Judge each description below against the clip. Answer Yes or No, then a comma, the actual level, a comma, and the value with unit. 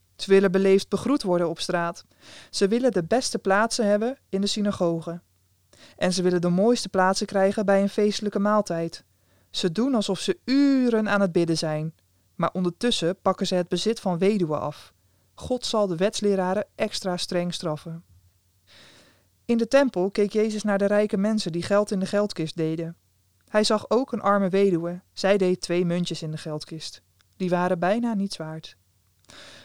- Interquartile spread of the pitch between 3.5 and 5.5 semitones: Yes, average, 4.0 semitones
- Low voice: No, medium, 185 Hz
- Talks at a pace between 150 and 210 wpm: Yes, average, 170 wpm